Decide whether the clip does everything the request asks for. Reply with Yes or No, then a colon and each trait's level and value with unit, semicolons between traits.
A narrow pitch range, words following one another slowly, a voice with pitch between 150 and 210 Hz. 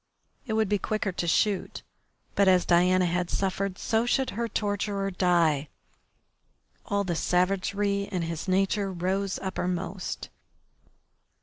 Yes: narrow, 2.1 semitones; slow, 125 wpm; high, 190 Hz